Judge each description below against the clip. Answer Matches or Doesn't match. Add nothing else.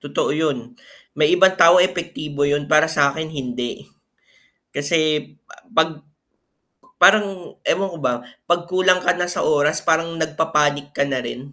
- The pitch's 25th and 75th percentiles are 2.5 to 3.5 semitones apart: Matches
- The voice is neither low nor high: Matches